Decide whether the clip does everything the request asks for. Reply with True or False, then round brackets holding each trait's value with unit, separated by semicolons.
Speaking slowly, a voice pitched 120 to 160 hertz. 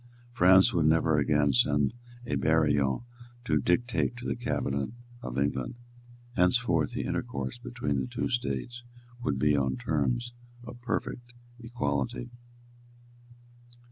False (120 wpm; 80 Hz)